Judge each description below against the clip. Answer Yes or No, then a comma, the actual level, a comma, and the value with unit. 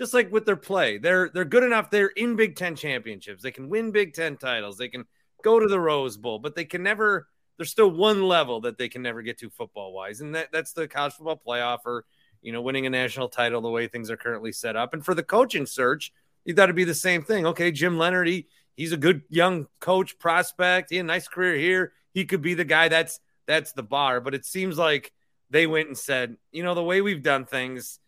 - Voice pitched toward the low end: No, medium, 165 Hz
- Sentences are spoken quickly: Yes, fast, 245 wpm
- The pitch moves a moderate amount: No, wide, 6.1 semitones